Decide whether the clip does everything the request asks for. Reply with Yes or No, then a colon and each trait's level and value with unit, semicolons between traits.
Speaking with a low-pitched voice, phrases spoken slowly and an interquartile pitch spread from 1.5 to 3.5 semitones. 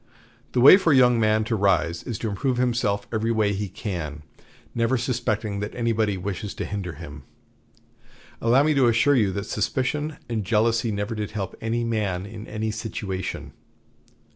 No: low, 110 Hz; average, 170 wpm; average, 2.8 semitones